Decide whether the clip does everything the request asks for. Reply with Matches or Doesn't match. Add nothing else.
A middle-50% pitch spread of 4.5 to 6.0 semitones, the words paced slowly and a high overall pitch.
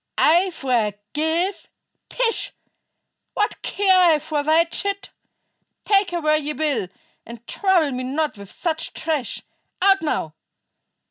Matches